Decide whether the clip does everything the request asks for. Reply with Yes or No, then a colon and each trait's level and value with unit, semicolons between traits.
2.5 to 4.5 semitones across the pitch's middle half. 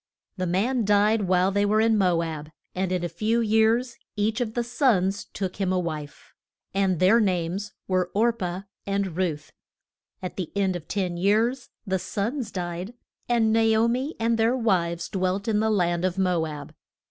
Yes: average, 3.7 semitones